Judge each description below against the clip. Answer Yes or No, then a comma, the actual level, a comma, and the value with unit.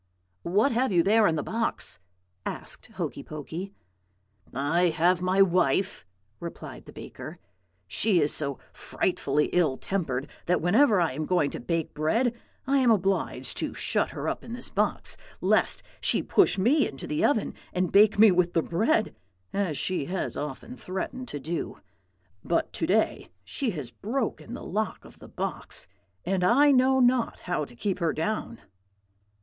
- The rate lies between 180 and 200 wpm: No, average, 165 wpm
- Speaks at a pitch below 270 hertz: Yes, medium, 185 Hz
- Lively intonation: Yes, wide, 5.9 semitones